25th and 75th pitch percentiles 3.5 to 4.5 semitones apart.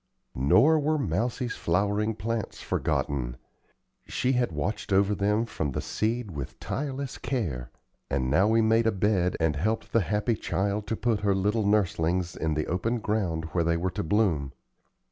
No: average, 5.1 semitones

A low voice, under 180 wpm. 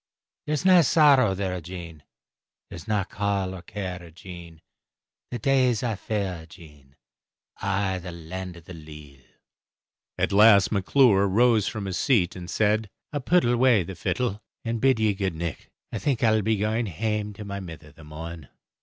Yes: low, 100 Hz; average, 170 wpm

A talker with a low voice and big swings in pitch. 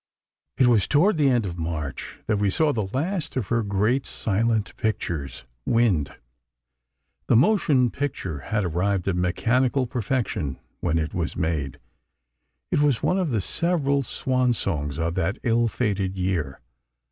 Yes: low, 110 Hz; wide, 6.6 semitones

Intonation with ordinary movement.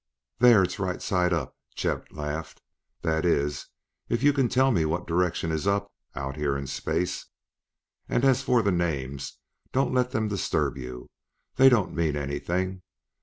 No: wide, 6.7 semitones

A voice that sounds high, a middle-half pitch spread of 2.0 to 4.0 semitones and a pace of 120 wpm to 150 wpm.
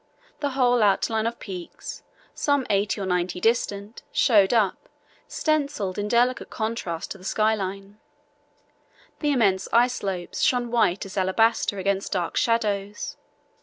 Yes: high, 210 Hz; average, 3.5 semitones; slow, 135 wpm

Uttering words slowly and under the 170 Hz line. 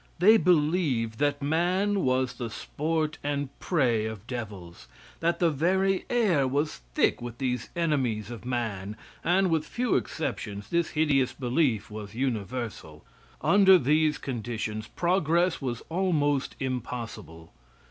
Yes: slow, 125 wpm; low, 135 Hz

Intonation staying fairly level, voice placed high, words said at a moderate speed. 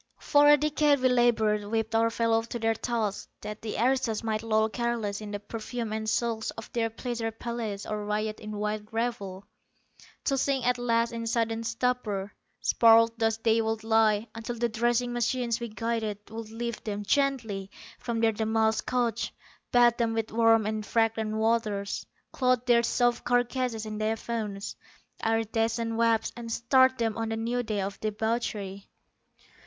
Yes: narrow, 1.6 semitones; high, 225 Hz; average, 165 wpm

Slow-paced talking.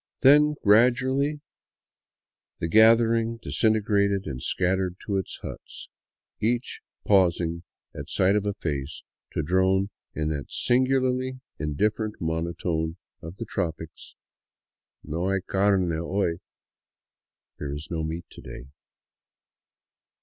Yes: slow, 120 wpm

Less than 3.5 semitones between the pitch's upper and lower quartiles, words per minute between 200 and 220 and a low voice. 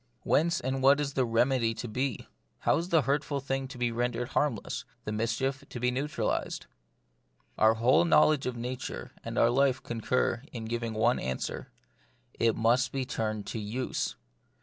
No: average, 2.9 semitones; average, 170 wpm; low, 125 Hz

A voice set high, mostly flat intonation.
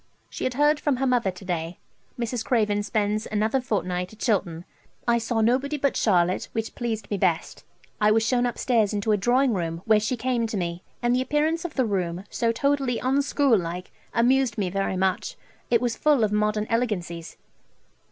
No: high, 225 Hz; average, 4.3 semitones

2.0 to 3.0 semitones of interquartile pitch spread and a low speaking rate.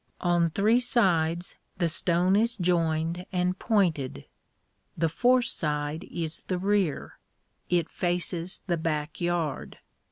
Yes: narrow, 2.6 semitones; slow, 120 wpm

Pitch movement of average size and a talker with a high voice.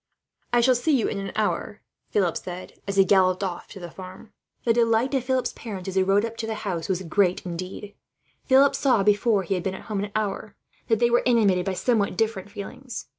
Yes: average, 3.4 semitones; high, 205 Hz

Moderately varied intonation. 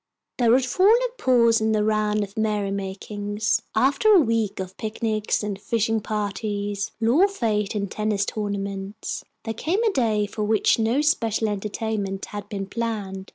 No: narrow, 2.1 semitones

